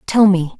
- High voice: Yes, high, 195 Hz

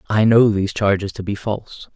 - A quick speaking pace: Yes, fast, 215 wpm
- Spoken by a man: Yes, male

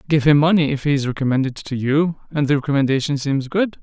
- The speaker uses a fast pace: Yes, fast, 220 wpm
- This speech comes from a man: Yes, male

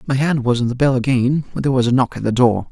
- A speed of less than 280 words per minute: No, fast, 330 wpm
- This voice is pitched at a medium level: No, low, 125 Hz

